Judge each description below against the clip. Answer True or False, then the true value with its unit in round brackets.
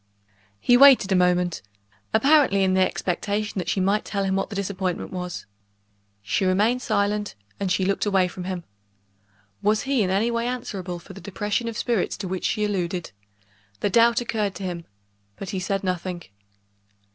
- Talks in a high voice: True (195 Hz)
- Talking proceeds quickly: False (175 wpm)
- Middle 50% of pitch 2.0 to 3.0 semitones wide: True (2.6 semitones)